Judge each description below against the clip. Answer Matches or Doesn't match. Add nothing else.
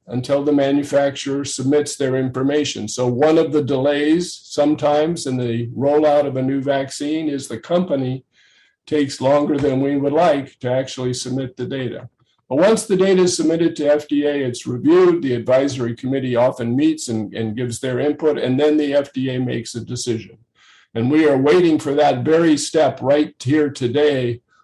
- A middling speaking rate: Matches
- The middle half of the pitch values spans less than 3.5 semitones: Matches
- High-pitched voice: Doesn't match